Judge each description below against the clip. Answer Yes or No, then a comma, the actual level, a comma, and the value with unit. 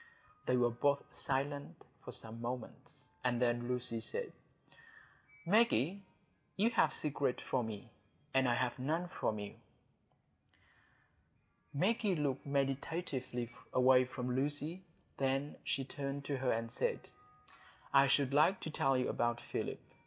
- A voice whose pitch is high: No, low, 135 Hz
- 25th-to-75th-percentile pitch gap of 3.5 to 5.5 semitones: No, average, 2.9 semitones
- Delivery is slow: Yes, slow, 130 wpm